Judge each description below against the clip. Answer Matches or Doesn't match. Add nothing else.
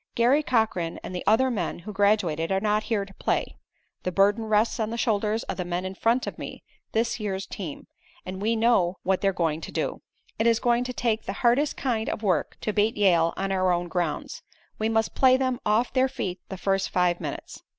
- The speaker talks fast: Matches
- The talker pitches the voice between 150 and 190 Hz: Doesn't match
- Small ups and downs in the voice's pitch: Doesn't match